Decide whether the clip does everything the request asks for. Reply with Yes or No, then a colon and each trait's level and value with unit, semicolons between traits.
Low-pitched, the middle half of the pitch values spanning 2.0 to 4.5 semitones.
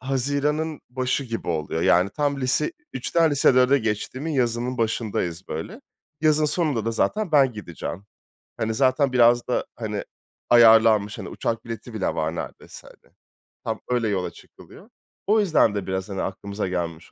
No: low, 115 Hz; average, 5.3 semitones